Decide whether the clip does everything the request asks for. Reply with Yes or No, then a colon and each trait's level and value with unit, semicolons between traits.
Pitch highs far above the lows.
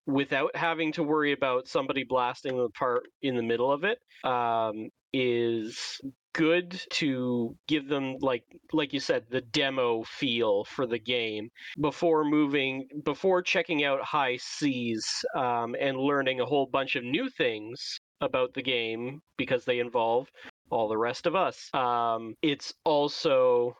No: average, 3.9 semitones